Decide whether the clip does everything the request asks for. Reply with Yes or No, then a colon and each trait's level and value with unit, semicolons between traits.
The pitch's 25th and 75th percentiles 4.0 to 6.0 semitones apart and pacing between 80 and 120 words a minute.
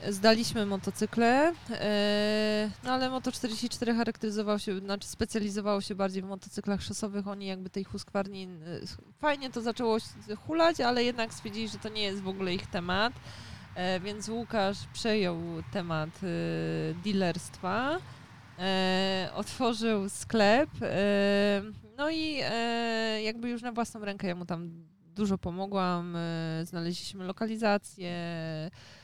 No: average, 3.5 semitones; slow, 110 wpm